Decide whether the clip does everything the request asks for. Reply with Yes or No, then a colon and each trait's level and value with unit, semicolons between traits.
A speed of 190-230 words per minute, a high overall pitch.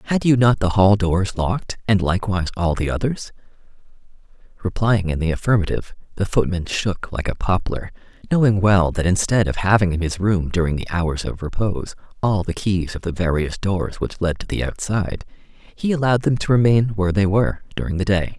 No: average, 195 wpm; very low, 95 Hz